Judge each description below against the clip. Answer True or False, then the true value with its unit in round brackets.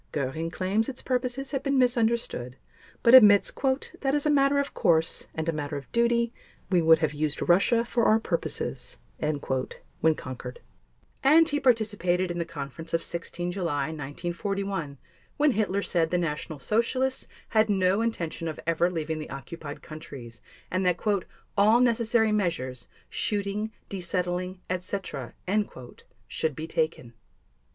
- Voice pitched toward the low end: False (180 Hz)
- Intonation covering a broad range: True (6.3 semitones)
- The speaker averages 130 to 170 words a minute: True (140 wpm)